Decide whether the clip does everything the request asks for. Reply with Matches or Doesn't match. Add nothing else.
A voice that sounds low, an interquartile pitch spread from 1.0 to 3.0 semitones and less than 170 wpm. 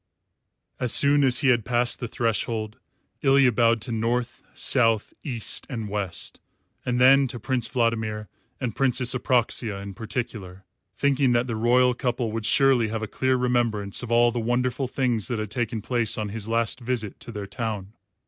Doesn't match